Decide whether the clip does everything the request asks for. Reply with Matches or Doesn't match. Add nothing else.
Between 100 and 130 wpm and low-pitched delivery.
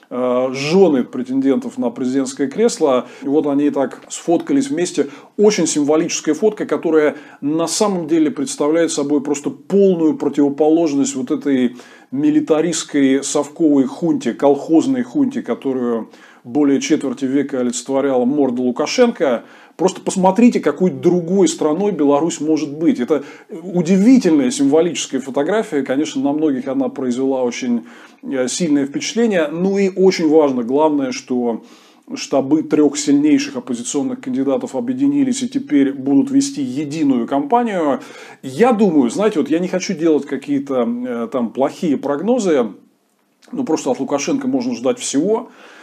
Doesn't match